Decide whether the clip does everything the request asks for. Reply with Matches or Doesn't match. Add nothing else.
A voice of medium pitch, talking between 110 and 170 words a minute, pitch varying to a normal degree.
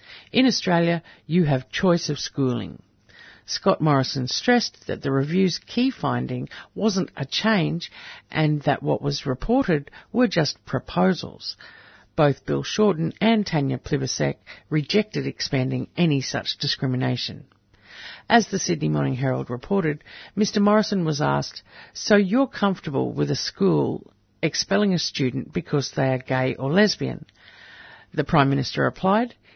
Doesn't match